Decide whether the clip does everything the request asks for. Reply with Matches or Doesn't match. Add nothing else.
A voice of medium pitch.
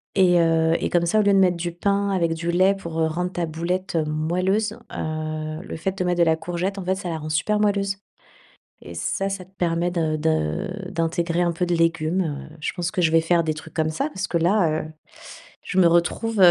Matches